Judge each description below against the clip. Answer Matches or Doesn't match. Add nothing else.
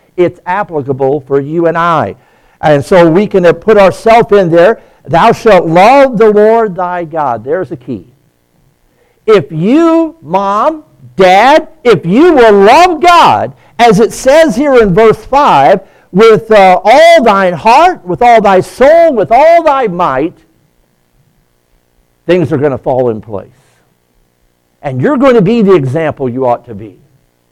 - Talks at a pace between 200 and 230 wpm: Doesn't match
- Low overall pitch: Doesn't match